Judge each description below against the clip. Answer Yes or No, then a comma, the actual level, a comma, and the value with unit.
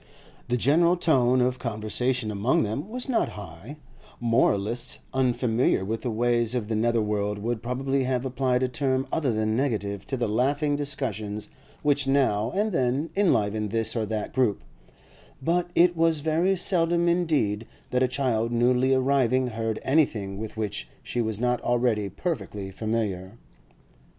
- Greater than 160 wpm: No, average, 155 wpm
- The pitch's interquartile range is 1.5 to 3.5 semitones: No, average, 4.2 semitones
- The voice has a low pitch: Yes, low, 125 Hz